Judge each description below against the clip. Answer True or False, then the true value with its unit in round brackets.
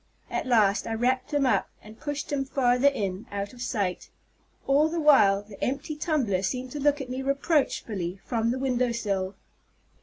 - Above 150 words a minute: True (180 wpm)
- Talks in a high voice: True (250 Hz)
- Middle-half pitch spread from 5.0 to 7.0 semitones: True (5.3 semitones)